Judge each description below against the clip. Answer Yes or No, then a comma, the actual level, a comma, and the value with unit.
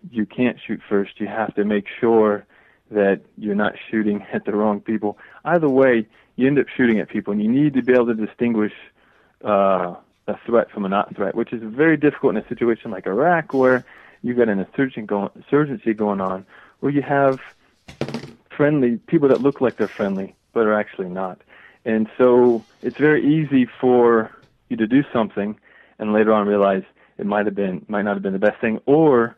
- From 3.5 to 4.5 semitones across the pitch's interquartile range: Yes, average, 3.8 semitones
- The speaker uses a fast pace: No, average, 195 wpm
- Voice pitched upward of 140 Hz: No, low, 110 Hz